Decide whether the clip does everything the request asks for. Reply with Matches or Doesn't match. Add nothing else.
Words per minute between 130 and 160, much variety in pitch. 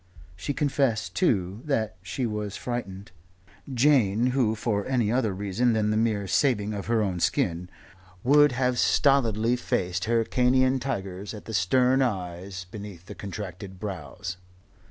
Doesn't match